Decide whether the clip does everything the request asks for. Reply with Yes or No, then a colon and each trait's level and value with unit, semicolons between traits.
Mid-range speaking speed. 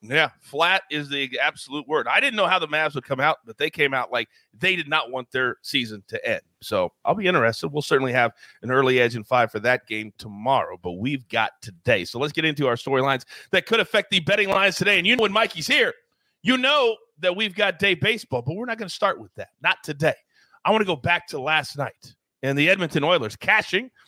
No: fast, 240 wpm